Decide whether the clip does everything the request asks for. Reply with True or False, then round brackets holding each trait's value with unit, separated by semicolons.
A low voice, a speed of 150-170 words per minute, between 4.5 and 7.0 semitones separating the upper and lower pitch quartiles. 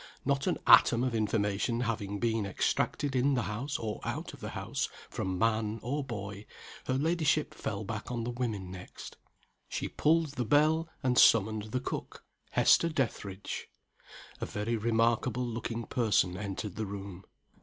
False (115 Hz; 155 wpm; 3.7 semitones)